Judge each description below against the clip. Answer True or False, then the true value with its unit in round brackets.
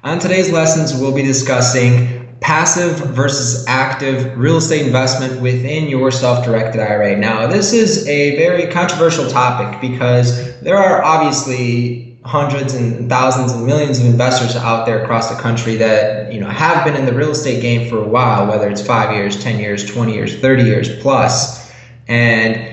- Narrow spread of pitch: False (3.3 semitones)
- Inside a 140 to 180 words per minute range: True (170 wpm)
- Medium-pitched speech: False (125 Hz)